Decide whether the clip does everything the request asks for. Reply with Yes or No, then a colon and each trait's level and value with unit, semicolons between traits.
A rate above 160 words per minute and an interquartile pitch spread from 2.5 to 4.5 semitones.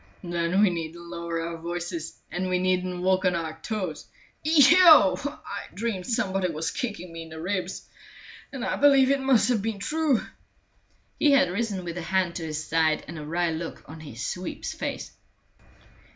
No: average, 180 wpm; average, 5.1 semitones